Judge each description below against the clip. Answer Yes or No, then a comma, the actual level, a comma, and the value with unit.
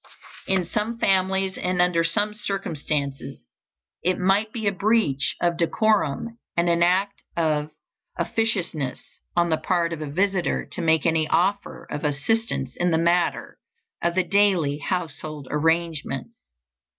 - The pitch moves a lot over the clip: No, average, 3.9 semitones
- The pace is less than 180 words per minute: Yes, average, 140 wpm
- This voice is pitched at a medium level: Yes, medium, 175 Hz